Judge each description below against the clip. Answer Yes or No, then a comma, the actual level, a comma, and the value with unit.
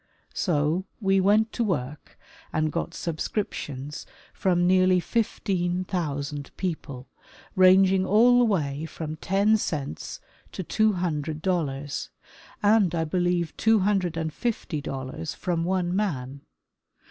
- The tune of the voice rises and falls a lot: No, average, 4.1 semitones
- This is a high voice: No, medium, 175 Hz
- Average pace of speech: No, slow, 125 wpm